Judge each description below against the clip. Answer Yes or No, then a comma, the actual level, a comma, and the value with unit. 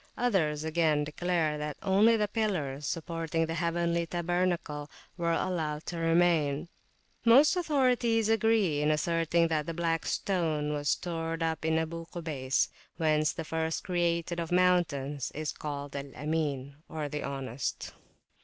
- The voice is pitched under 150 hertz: No, medium, 165 Hz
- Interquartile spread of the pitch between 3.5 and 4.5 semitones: No, average, 2.7 semitones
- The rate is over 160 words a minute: No, slow, 135 wpm